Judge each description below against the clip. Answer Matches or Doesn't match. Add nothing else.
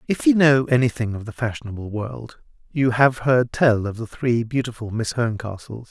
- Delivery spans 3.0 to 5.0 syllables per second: Matches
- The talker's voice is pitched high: Doesn't match